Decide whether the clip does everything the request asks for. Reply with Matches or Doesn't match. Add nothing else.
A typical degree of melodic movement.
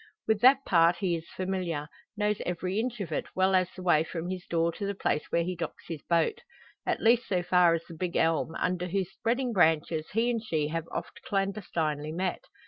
Matches